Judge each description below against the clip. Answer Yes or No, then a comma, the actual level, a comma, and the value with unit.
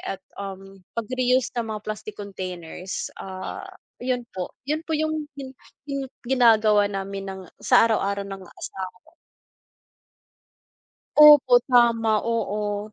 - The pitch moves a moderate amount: Yes, average, 4.0 semitones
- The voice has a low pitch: No, high, 215 Hz